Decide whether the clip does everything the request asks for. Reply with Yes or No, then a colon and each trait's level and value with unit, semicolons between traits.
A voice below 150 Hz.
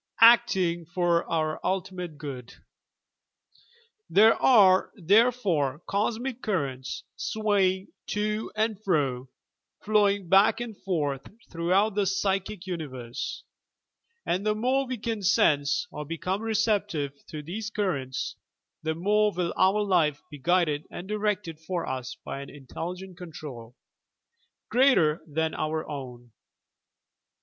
No: medium, 180 Hz